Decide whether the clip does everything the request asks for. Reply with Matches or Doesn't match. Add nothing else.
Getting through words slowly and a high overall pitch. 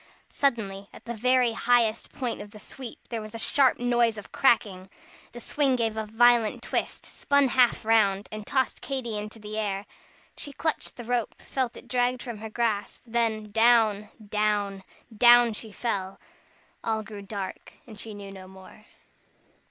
Doesn't match